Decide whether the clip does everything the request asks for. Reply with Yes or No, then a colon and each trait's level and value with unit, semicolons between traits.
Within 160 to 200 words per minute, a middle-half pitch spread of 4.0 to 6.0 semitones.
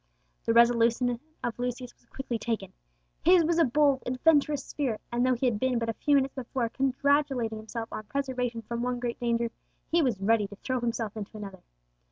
No: average, 195 wpm; average, 2.8 semitones